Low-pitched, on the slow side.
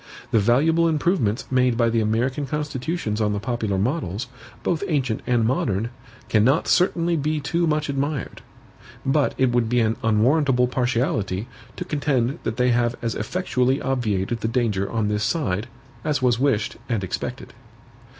No: low, 125 Hz; average, 155 wpm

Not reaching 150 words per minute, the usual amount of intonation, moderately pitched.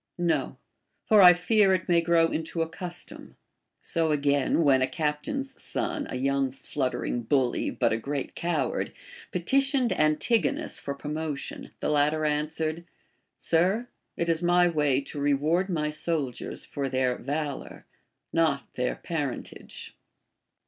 Yes: slow, 135 wpm; average, 3.7 semitones; medium, 155 Hz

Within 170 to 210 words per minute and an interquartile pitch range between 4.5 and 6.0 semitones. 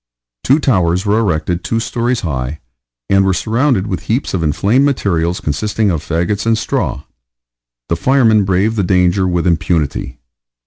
No: average, 150 wpm; average, 5.0 semitones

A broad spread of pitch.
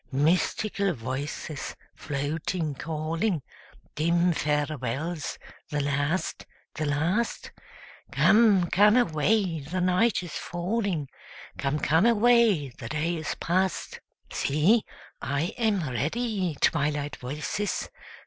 No: average, 4.8 semitones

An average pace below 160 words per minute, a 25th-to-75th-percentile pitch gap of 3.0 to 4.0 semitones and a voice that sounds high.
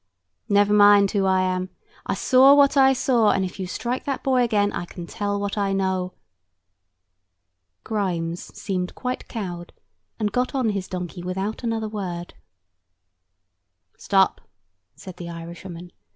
Yes: average, 145 wpm; average, 3.5 semitones; high, 200 Hz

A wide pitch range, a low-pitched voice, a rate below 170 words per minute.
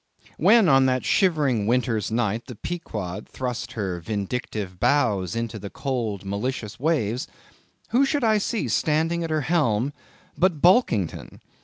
Yes: wide, 7.2 semitones; low, 125 Hz; average, 140 wpm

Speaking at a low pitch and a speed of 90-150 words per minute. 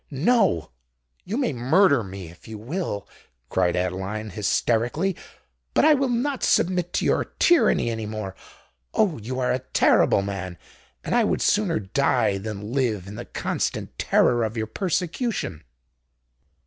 Yes: low, 115 Hz; average, 140 wpm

